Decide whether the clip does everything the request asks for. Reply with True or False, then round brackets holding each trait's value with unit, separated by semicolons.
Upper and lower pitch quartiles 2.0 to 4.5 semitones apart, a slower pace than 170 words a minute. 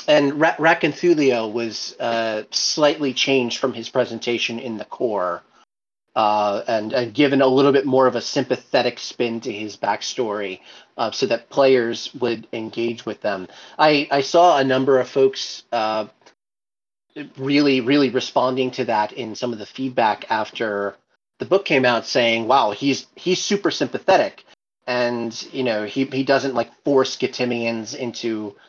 True (3.1 semitones; 155 wpm)